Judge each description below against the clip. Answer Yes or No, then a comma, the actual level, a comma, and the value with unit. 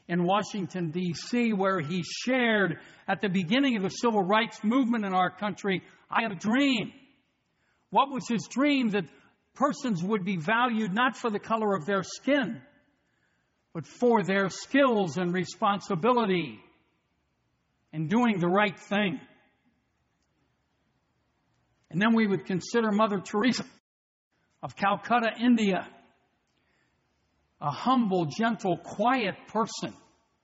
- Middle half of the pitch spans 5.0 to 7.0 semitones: No, average, 4.1 semitones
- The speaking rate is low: Yes, slow, 125 wpm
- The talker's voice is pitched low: No, high, 205 Hz